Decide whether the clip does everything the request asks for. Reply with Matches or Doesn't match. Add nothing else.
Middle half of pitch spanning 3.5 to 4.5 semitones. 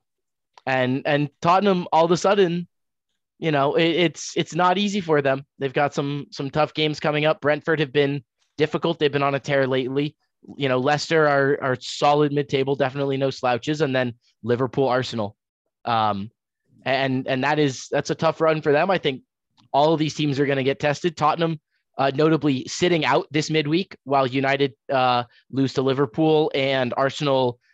Doesn't match